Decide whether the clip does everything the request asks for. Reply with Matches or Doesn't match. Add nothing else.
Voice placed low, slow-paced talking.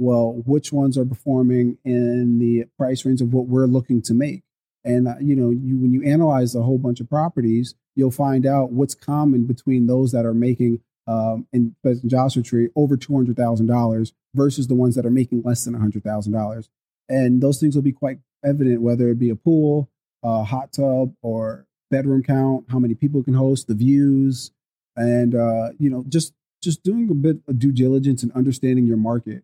Doesn't match